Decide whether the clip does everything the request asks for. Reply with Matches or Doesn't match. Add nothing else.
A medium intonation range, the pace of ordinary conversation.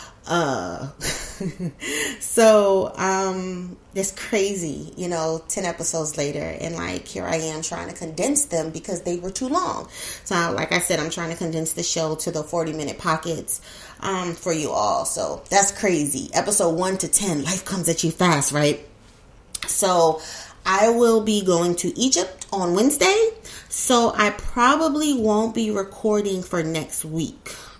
Matches